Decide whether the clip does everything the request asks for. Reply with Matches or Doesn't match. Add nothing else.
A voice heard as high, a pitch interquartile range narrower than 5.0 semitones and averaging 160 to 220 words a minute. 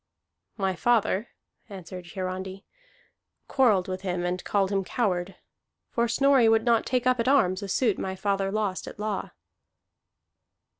Doesn't match